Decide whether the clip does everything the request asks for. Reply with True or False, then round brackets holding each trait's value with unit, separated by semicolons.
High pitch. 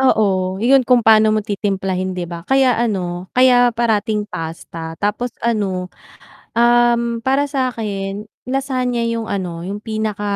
True (215 Hz)